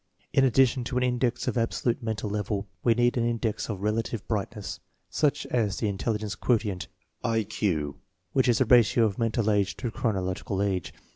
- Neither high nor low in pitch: No, low, 110 Hz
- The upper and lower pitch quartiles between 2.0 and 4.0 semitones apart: Yes, average, 3.1 semitones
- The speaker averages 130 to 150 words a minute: No, average, 185 wpm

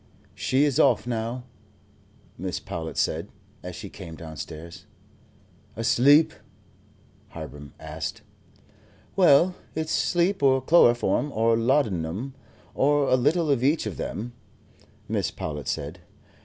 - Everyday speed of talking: No, slow, 115 wpm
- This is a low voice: Yes, low, 125 Hz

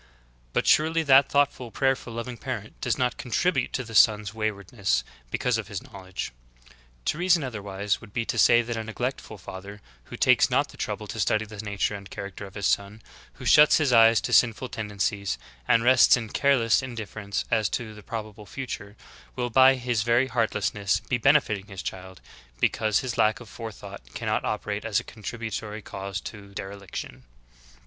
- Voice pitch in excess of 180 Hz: No, low, 110 Hz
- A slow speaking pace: No, average, 180 wpm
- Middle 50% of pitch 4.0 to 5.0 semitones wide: No, average, 3.4 semitones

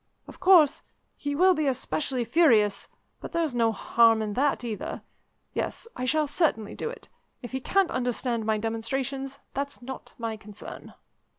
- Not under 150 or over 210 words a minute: Yes, average, 160 wpm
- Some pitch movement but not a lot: Yes, average, 4.5 semitones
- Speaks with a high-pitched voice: Yes, very high, 255 Hz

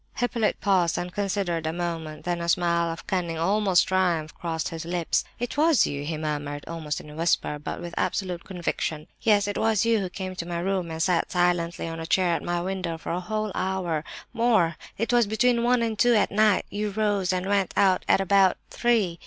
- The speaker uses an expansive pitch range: No, average, 3.5 semitones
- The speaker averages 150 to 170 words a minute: No, average, 200 wpm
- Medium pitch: Yes, medium, 180 Hz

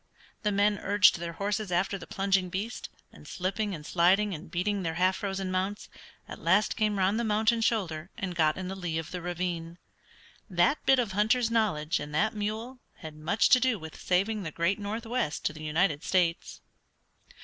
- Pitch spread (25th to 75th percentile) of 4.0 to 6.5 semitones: No, average, 3.6 semitones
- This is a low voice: No, high, 190 Hz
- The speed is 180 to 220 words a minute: Yes, average, 190 wpm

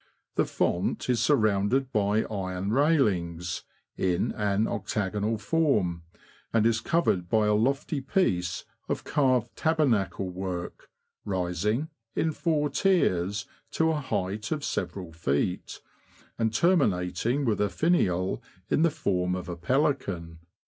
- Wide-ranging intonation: Yes, wide, 7.3 semitones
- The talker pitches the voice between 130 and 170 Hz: No, low, 105 Hz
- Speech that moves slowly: Yes, slow, 125 wpm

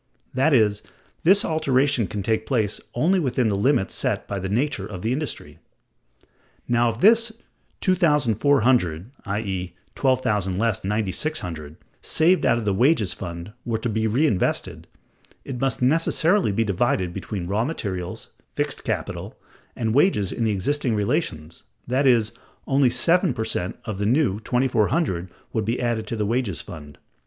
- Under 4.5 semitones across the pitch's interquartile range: No, wide, 5.5 semitones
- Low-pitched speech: Yes, low, 115 Hz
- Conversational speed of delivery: Yes, average, 150 wpm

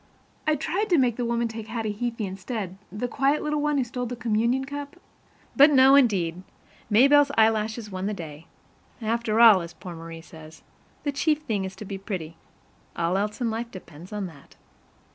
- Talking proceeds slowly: No, average, 185 wpm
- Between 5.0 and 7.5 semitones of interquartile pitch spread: Yes, wide, 5.4 semitones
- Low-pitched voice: No, high, 225 Hz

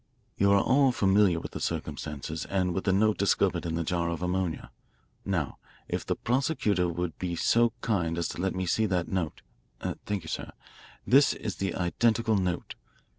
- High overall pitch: No, very low, 95 Hz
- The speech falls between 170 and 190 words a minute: Yes, average, 180 wpm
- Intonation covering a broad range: No, average, 3.5 semitones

